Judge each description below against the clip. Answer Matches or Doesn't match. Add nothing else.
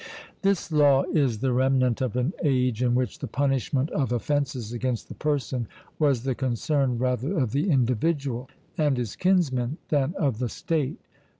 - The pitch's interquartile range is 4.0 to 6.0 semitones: Doesn't match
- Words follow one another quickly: Doesn't match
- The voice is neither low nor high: Doesn't match